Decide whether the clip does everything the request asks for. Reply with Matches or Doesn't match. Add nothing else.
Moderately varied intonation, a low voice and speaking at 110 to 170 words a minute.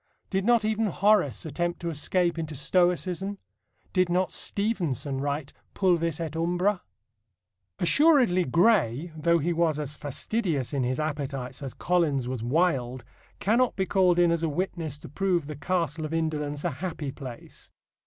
Doesn't match